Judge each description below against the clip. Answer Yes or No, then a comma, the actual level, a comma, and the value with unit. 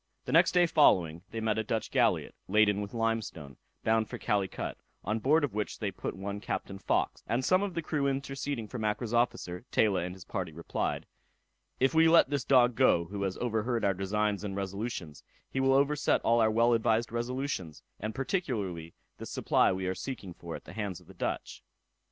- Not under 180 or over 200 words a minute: Yes, average, 195 wpm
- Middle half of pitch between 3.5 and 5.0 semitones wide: Yes, average, 4.7 semitones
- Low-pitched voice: Yes, low, 110 Hz